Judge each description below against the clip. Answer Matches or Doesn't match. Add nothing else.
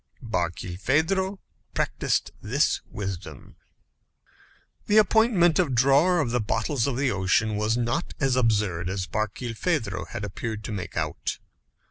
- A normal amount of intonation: Doesn't match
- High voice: Doesn't match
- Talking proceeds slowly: Matches